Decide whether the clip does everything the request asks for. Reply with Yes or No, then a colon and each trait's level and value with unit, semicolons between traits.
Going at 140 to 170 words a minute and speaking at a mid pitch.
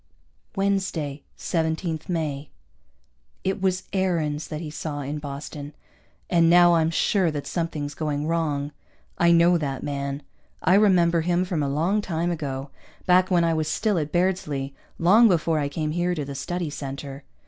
Yes: average, 160 wpm; medium, 160 Hz